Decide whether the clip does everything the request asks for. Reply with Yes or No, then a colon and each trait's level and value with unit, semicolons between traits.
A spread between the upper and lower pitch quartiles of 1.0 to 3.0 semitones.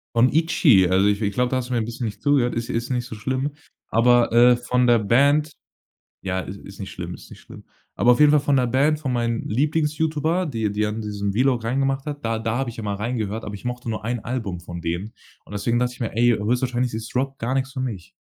No: average, 3.5 semitones